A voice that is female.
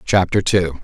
No: male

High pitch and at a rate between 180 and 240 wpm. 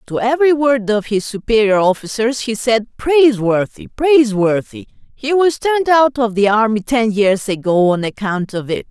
No: high, 230 Hz; average, 170 wpm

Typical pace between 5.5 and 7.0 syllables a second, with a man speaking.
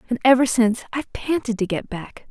No: 6.1 syllables/s; female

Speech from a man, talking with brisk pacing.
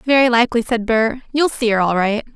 No: female; fast, 230 wpm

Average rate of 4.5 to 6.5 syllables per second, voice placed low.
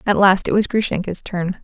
No: 5.3 syllables/s; high, 190 Hz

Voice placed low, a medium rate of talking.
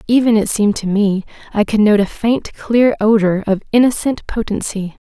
No: high, 215 Hz; average, 175 wpm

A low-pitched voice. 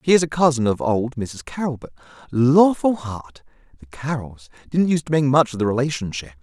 Yes: low, 130 Hz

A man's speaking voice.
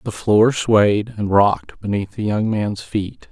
Yes: male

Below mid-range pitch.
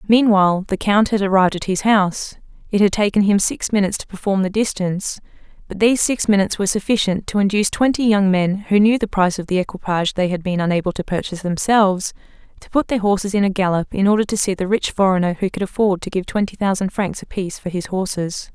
No: high, 195 Hz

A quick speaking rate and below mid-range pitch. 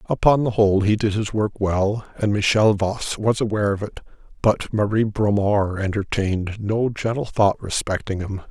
No: average, 170 wpm; low, 105 Hz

